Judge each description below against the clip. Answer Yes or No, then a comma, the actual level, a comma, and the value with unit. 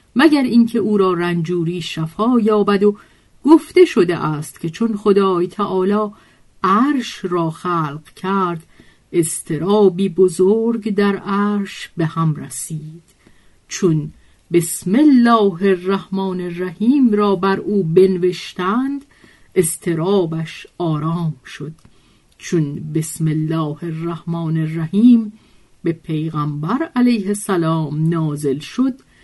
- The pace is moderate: No, slow, 100 wpm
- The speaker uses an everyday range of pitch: Yes, average, 4.1 semitones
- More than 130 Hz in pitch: Yes, medium, 185 Hz